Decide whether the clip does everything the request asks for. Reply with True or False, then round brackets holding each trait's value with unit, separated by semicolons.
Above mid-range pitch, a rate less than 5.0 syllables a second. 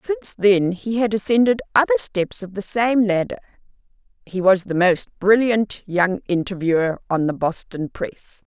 True (200 Hz; 4.6 syllables/s)